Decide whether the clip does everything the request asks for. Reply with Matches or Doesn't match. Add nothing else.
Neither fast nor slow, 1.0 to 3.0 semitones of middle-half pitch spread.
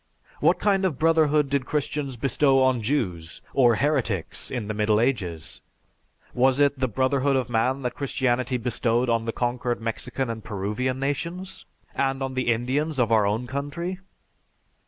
Doesn't match